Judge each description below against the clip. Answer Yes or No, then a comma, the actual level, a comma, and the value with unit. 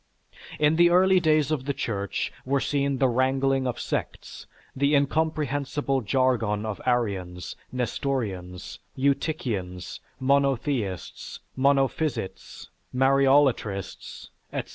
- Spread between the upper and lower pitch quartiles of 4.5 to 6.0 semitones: No, average, 3.9 semitones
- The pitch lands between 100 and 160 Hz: Yes, low, 135 Hz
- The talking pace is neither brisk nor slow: No, slow, 100 wpm